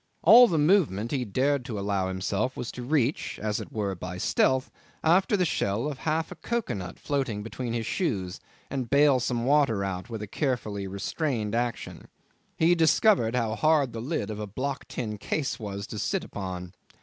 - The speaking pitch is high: No, low, 120 Hz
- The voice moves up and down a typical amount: No, wide, 6.2 semitones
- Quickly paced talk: No, average, 195 wpm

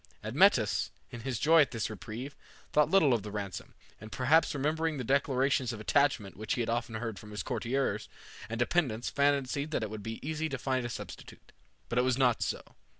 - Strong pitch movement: No, average, 4.0 semitones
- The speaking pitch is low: Yes, low, 125 Hz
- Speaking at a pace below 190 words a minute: No, fast, 205 wpm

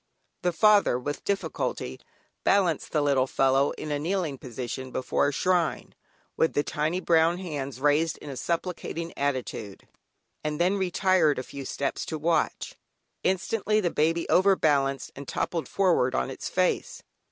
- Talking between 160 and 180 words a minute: No, average, 150 wpm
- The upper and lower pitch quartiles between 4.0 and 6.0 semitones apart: Yes, average, 4.5 semitones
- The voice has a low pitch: No, medium, 155 Hz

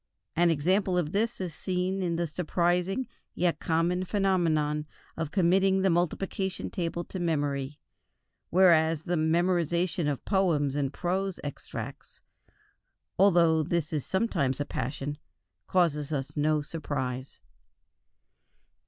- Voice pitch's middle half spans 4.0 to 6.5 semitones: No, average, 3.6 semitones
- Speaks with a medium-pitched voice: Yes, medium, 170 Hz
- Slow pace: Yes, slow, 120 wpm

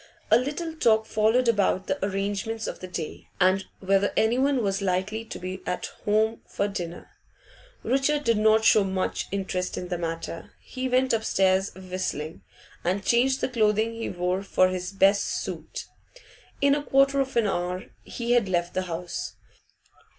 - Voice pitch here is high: Yes, high, 200 Hz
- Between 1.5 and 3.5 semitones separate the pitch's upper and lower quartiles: No, average, 3.9 semitones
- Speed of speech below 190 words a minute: Yes, average, 165 wpm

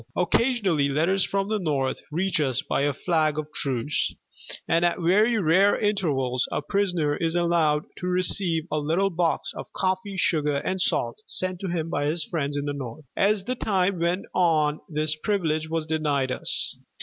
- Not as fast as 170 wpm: No, average, 175 wpm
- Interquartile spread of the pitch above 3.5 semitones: Yes, average, 3.9 semitones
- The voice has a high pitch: No, medium, 165 Hz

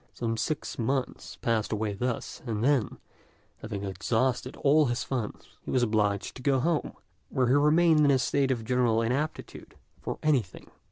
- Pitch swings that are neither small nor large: Yes, average, 4.0 semitones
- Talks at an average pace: Yes, average, 165 wpm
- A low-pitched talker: Yes, low, 125 Hz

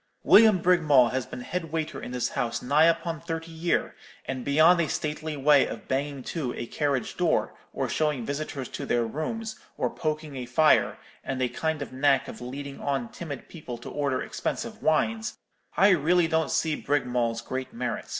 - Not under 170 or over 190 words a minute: Yes, average, 180 wpm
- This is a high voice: No, medium, 145 Hz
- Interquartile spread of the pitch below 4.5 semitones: Yes, average, 3.8 semitones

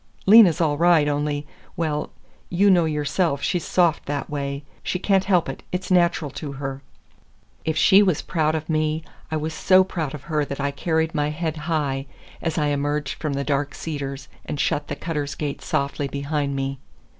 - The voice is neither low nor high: Yes, medium, 150 Hz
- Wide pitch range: No, average, 2.7 semitones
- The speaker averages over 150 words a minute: Yes, average, 180 wpm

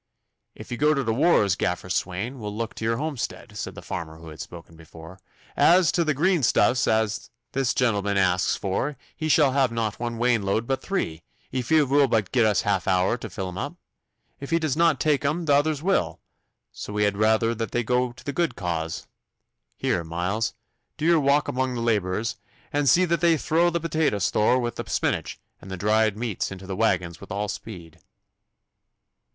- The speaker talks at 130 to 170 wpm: No, average, 200 wpm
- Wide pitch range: Yes, wide, 6.6 semitones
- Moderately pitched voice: No, low, 115 Hz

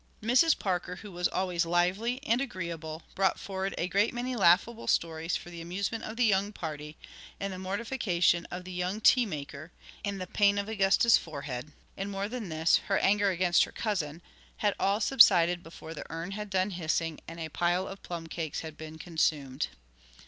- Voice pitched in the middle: Yes, medium, 180 Hz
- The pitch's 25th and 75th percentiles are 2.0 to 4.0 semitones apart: Yes, average, 3.6 semitones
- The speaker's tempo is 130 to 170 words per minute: No, average, 185 wpm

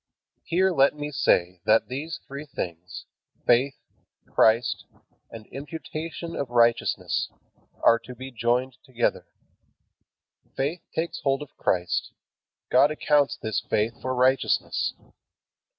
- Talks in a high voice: No, low, 130 Hz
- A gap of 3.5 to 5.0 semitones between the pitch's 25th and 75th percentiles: Yes, average, 4.0 semitones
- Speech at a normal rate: No, slow, 115 wpm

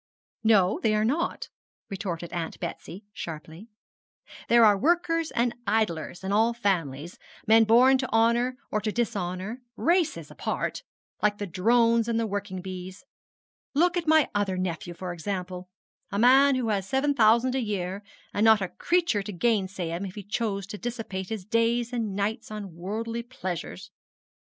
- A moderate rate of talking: Yes, average, 160 wpm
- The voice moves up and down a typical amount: Yes, average, 4.0 semitones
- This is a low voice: No, high, 210 Hz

